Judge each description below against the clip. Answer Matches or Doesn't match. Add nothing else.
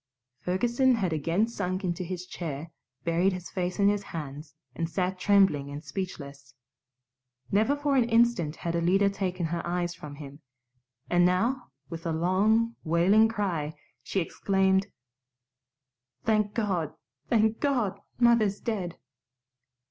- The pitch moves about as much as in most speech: Matches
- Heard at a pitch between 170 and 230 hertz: Matches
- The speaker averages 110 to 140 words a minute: Matches